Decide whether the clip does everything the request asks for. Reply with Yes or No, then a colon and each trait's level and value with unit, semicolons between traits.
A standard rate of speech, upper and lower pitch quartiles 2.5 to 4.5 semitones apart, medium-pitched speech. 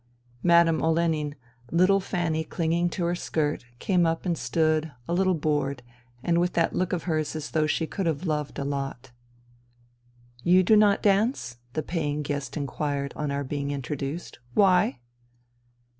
Yes: average, 170 wpm; average, 3.5 semitones; medium, 155 Hz